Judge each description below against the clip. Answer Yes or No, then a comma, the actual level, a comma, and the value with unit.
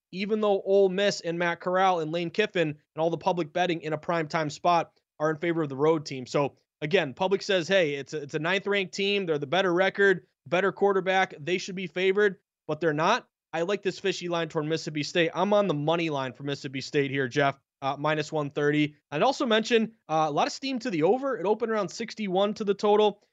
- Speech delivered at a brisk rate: Yes, fast, 230 wpm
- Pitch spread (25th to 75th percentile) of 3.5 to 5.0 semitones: Yes, average, 4.3 semitones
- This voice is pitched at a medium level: Yes, medium, 175 Hz